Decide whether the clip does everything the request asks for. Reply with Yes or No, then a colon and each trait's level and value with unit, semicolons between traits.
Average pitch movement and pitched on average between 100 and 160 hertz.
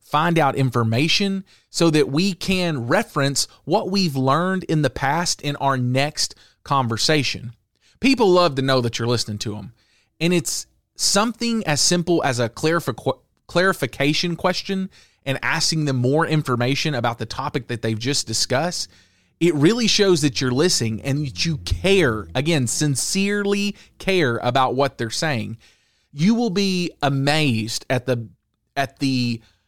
No: wide, 6.1 semitones; medium, 140 Hz